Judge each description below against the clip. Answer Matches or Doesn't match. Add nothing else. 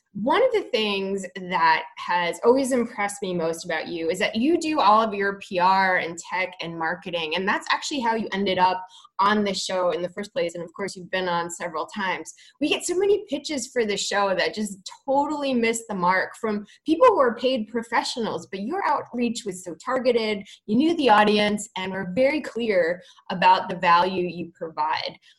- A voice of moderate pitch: Doesn't match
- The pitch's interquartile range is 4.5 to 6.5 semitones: Matches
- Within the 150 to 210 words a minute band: Matches